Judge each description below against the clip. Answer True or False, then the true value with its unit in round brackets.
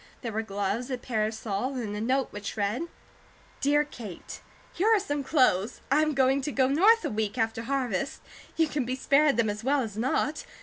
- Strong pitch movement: False (4.6 semitones)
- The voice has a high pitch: True (255 Hz)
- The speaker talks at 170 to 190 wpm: False (200 wpm)